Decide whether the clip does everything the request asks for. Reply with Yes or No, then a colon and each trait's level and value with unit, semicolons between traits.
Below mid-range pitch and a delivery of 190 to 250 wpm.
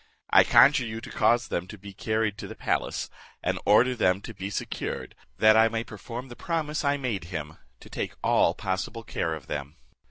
Yes: low, 110 Hz; average, 200 wpm